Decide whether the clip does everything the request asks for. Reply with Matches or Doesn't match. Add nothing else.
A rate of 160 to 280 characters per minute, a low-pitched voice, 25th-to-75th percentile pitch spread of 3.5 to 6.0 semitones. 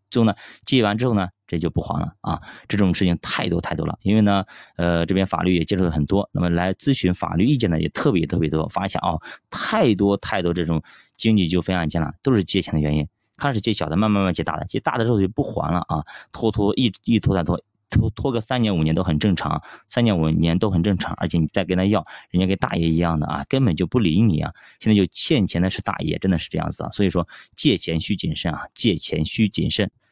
Doesn't match